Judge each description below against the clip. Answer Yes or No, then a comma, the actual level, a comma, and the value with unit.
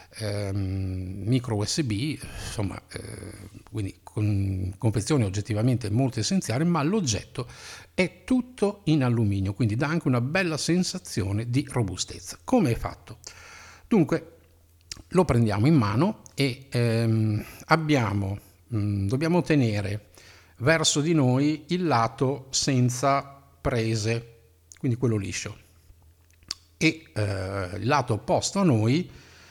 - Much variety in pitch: Yes, wide, 5.9 semitones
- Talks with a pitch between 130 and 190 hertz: No, low, 110 Hz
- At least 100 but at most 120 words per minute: Yes, slow, 115 wpm